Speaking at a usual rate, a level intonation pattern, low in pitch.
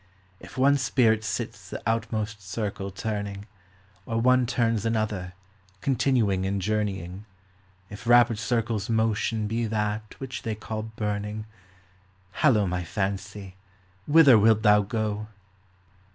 No: slow, 120 wpm; narrow, 2.1 semitones; low, 110 Hz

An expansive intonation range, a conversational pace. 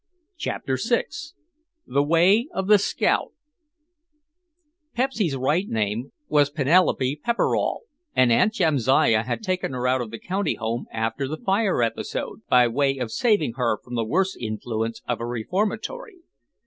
Yes: wide, 8.2 semitones; average, 145 wpm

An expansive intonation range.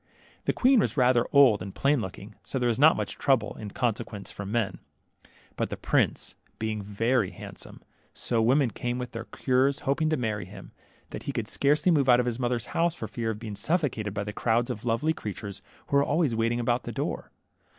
No: average, 4.1 semitones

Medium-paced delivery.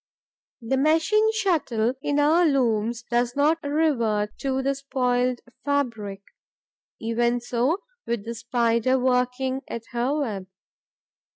No: slow, 115 wpm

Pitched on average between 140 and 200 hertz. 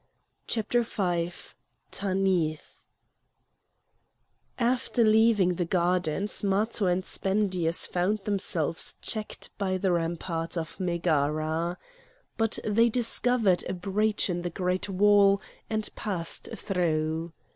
Yes: medium, 185 Hz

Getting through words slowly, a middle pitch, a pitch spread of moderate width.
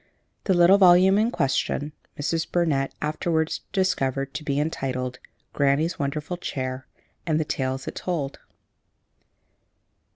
Yes: slow, 125 wpm; medium, 150 Hz; average, 4.2 semitones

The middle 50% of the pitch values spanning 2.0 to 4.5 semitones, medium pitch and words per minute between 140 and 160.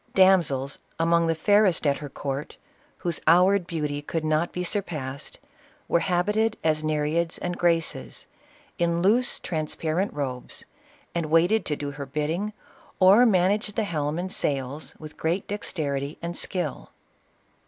Yes: average, 3.7 semitones; medium, 165 Hz; average, 145 wpm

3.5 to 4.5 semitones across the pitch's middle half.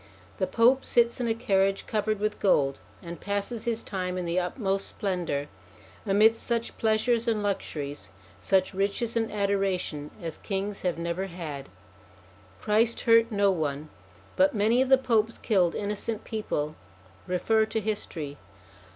Yes: average, 3.8 semitones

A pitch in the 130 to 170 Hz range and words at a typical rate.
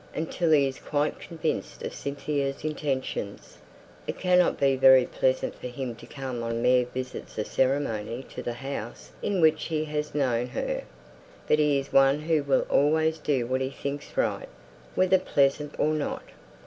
Yes: medium, 140 Hz; average, 160 wpm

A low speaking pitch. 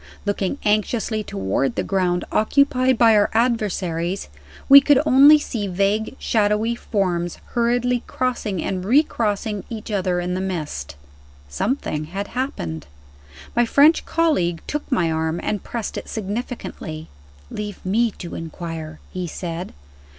No: high, 205 Hz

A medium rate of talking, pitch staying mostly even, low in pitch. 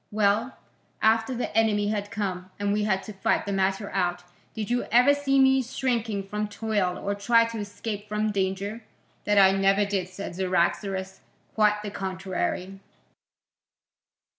No: average, 155 wpm; narrow, 2.3 semitones; high, 205 Hz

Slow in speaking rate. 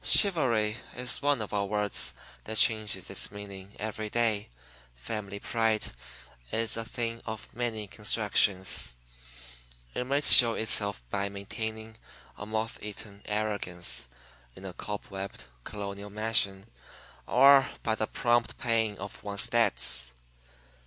Yes: slow, 125 wpm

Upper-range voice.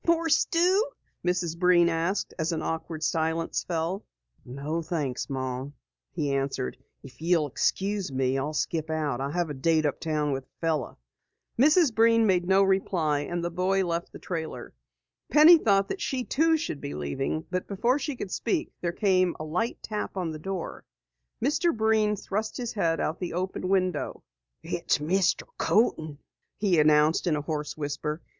No: medium, 170 Hz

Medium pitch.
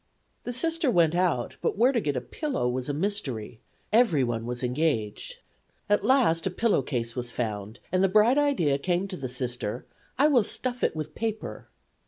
Yes: medium, 165 Hz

